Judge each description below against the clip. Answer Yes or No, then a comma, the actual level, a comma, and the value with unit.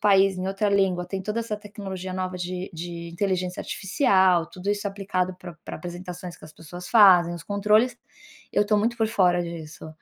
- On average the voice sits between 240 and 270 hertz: No, medium, 185 Hz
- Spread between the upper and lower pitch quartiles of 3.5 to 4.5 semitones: No, narrow, 2.5 semitones